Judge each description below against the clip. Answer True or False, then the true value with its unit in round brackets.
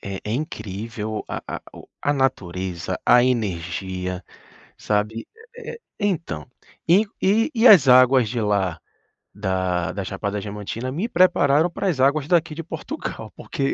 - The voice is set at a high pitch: False (115 Hz)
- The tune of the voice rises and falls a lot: True (8.0 semitones)